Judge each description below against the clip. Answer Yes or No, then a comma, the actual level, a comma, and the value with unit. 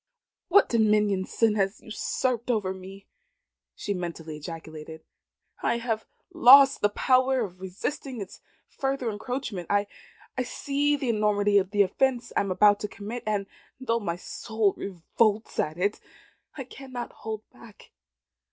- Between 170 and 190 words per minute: No, average, 140 wpm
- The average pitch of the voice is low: No, high, 210 Hz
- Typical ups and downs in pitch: Yes, average, 4.1 semitones